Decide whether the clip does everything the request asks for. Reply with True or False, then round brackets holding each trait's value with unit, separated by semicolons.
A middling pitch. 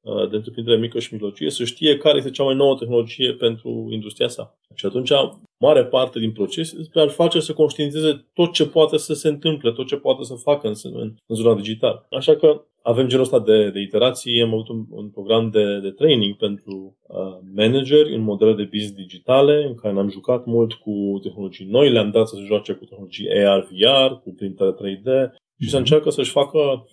False (115 Hz)